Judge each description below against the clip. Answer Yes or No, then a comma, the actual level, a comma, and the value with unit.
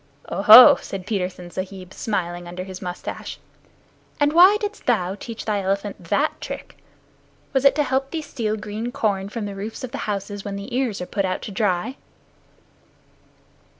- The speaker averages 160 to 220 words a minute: Yes, average, 170 wpm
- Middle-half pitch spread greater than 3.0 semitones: Yes, average, 4.5 semitones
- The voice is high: Yes, high, 205 Hz